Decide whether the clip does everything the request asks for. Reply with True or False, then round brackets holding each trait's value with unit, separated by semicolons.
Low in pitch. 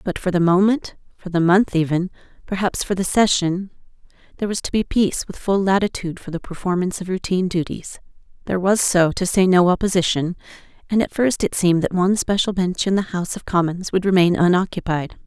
False (185 Hz)